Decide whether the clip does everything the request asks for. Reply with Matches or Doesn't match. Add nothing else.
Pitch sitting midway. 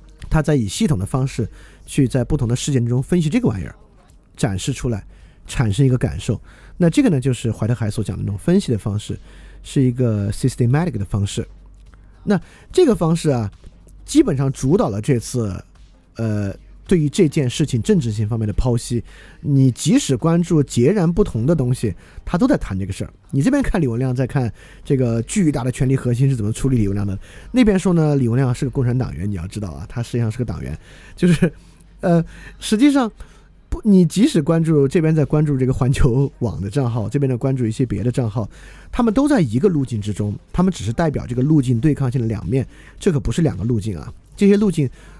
Doesn't match